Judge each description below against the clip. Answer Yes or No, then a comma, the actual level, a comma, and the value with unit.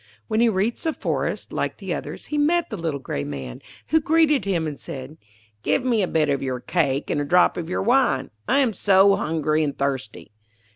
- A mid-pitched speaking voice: Yes, medium, 170 Hz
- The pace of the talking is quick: Yes, fast, 210 wpm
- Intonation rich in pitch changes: Yes, wide, 9.0 semitones